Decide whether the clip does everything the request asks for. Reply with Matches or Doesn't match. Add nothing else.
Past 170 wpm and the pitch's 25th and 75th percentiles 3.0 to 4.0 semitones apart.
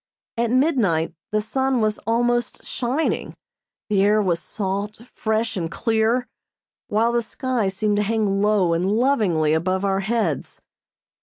Doesn't match